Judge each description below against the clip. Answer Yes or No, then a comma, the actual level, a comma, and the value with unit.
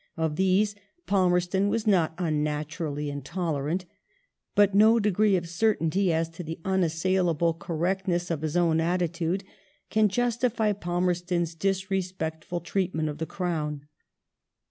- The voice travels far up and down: No, average, 3.0 semitones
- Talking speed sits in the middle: No, slow, 120 wpm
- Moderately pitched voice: Yes, medium, 175 Hz